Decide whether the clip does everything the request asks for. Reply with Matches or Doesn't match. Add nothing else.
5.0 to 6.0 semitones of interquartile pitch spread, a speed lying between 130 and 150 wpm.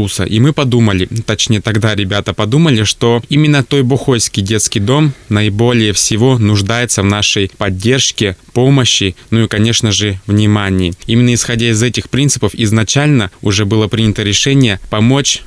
Doesn't match